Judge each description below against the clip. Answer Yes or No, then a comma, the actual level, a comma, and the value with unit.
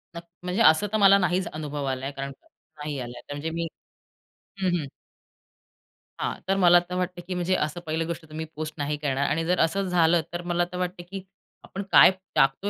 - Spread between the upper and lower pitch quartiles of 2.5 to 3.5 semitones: Yes, average, 3.2 semitones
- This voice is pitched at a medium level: Yes, medium, 170 Hz